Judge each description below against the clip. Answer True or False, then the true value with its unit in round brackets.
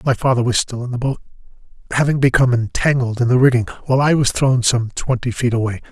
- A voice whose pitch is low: True (125 Hz)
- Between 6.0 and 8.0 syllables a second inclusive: True (6.5 syllables/s)